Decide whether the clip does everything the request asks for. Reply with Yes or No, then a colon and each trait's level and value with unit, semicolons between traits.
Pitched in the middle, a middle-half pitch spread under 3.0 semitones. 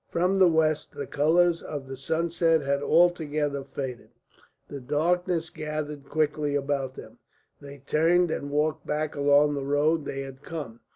Yes: medium, 150 Hz; narrow, 2.5 semitones